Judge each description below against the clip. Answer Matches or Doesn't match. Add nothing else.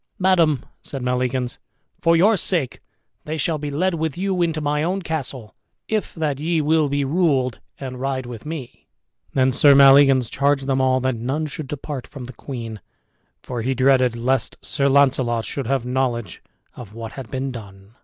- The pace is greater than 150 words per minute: Matches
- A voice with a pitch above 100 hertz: Matches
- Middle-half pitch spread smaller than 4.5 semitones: Matches